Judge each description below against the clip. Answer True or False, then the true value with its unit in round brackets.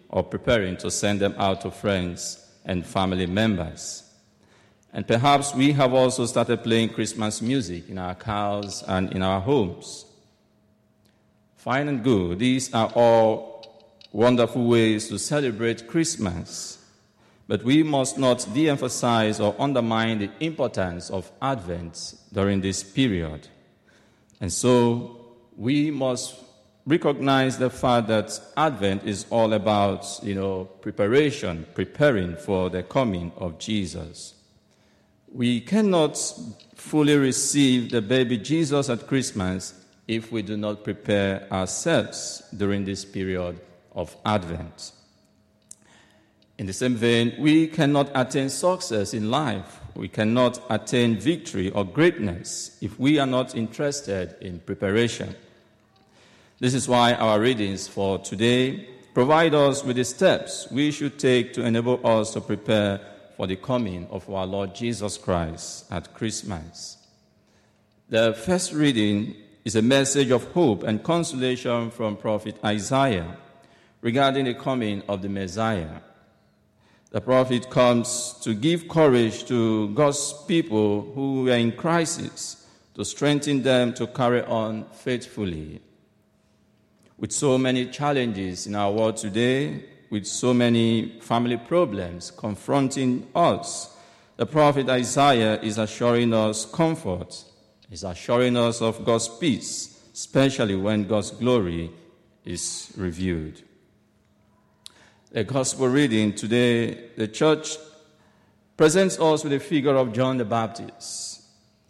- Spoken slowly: True (125 wpm)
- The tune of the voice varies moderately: True (4.1 semitones)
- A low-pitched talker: True (115 Hz)